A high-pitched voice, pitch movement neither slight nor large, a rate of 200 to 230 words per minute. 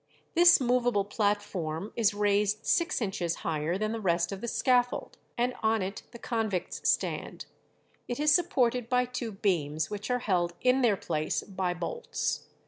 No: high, 210 Hz; average, 4.7 semitones; average, 160 wpm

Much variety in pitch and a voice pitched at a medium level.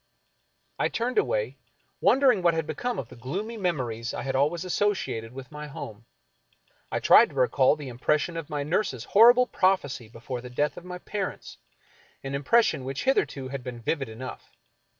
Yes: wide, 6.9 semitones; medium, 150 Hz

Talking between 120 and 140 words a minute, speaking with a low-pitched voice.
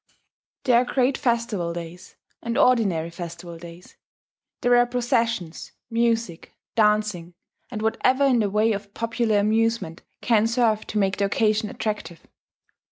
No: slow, 135 wpm; high, 215 Hz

